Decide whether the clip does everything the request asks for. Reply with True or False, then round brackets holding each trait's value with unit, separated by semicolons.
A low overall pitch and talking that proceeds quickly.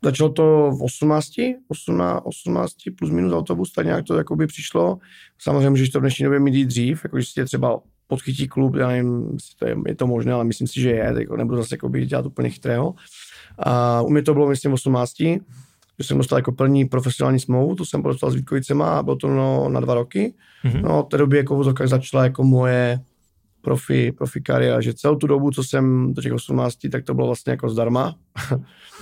True (130 Hz; 200 wpm)